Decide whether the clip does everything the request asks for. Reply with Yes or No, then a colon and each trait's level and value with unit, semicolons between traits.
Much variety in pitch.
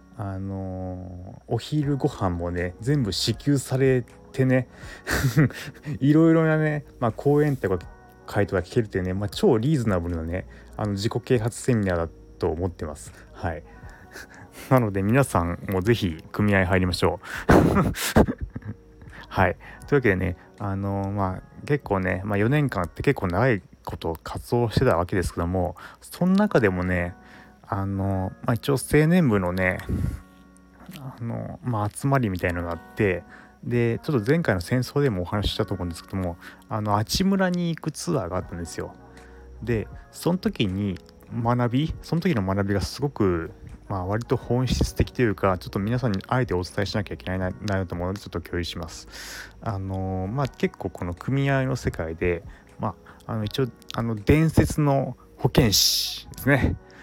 Yes: wide, 5.8 semitones